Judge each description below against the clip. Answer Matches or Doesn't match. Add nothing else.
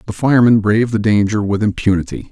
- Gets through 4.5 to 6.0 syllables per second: Doesn't match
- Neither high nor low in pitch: Doesn't match